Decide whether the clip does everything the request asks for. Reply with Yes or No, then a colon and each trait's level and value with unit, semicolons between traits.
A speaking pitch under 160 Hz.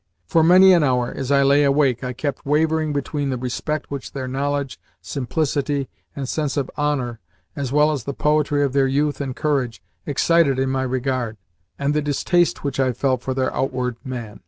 Yes: medium, 140 Hz